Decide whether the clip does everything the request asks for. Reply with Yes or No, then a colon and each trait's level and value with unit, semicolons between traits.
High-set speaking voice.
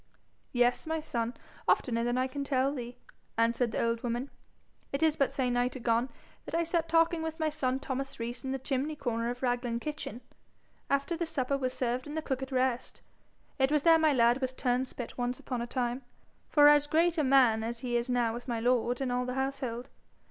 Yes: very high, 255 Hz